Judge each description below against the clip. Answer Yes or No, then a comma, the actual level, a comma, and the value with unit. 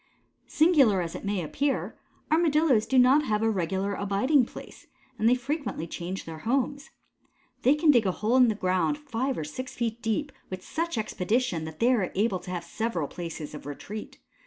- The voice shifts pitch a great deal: Yes, wide, 6.3 semitones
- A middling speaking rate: Yes, average, 185 wpm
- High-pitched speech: Yes, high, 225 Hz